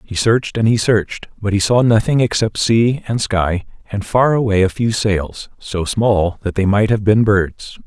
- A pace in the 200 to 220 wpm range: Yes, fast, 205 wpm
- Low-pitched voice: Yes, low, 105 Hz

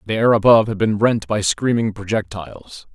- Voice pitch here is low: Yes, low, 105 Hz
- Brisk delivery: No, average, 185 wpm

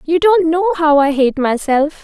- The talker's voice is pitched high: Yes, very high, 315 Hz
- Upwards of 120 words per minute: Yes, fast, 205 wpm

